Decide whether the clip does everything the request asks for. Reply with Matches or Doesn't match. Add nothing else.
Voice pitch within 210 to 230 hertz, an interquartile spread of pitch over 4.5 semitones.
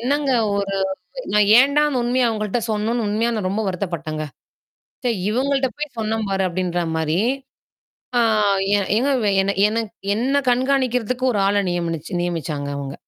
Matches